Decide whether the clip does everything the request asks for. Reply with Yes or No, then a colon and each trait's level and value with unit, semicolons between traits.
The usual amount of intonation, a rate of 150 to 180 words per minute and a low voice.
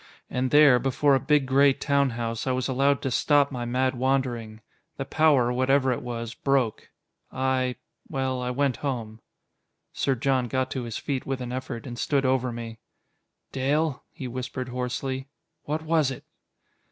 No: narrow, 1.8 semitones; average, 165 wpm; low, 130 Hz